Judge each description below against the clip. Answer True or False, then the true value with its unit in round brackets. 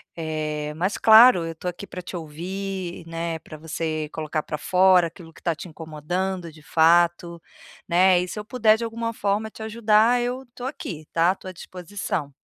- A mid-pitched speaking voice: True (175 Hz)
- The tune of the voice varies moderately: True (4.0 semitones)